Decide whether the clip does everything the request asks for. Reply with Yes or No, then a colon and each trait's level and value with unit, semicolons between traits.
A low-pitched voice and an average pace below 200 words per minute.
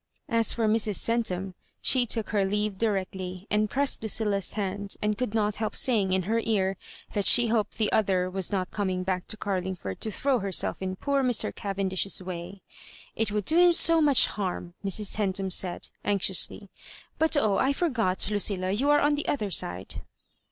No: high, 205 Hz; average, 190 wpm